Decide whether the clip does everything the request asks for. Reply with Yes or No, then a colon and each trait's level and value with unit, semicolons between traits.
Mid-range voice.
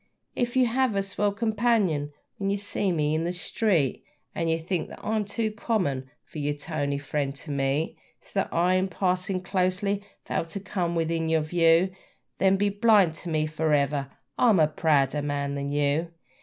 Yes: medium, 170 Hz